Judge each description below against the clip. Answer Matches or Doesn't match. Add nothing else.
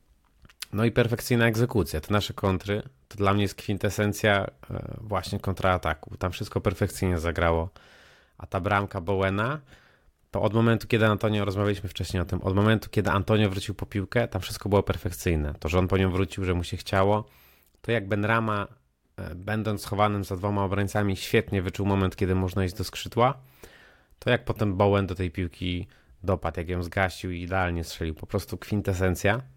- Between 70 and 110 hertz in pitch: Matches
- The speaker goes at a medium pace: Doesn't match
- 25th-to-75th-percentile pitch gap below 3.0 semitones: Matches